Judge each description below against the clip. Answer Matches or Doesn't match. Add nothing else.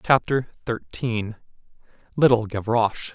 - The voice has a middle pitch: Doesn't match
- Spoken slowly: Matches